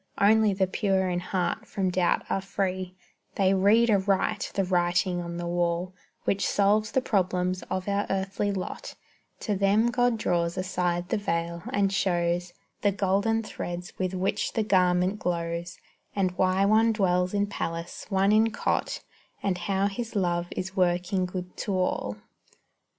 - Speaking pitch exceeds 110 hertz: Yes, high, 190 Hz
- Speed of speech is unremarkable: Yes, average, 155 wpm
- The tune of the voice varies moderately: No, narrow, 2.2 semitones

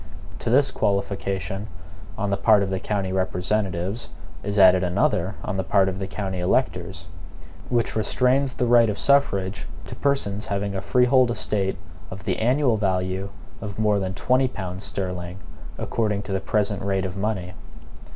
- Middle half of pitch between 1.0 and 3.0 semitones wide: Yes, narrow, 2.6 semitones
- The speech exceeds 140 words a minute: Yes, average, 160 wpm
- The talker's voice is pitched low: Yes, low, 100 Hz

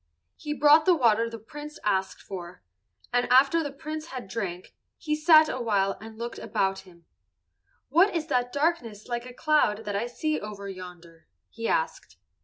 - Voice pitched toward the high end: Yes, high, 235 Hz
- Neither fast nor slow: Yes, average, 170 wpm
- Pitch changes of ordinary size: No, wide, 7.3 semitones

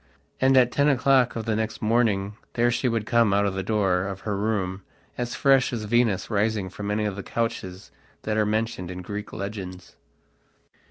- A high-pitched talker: No, low, 105 Hz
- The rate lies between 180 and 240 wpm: Yes, average, 185 wpm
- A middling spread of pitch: Yes, average, 3.0 semitones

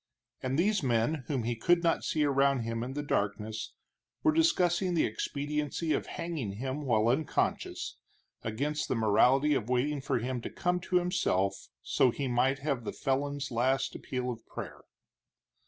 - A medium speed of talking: Yes, average, 165 wpm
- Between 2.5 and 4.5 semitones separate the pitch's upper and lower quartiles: Yes, average, 4.1 semitones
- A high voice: No, low, 135 Hz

